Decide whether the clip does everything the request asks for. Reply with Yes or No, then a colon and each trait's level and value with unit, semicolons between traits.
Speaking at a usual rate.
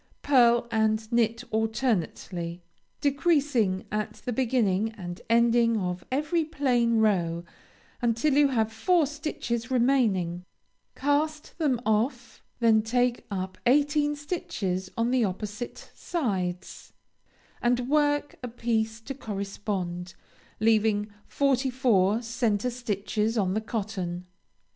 No: slow, 110 wpm